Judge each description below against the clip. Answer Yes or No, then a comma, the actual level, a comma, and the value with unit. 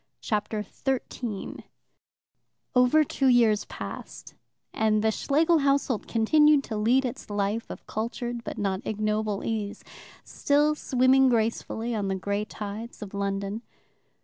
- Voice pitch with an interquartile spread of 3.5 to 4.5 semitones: Yes, average, 3.8 semitones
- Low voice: No, high, 225 Hz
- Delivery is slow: Yes, slow, 125 wpm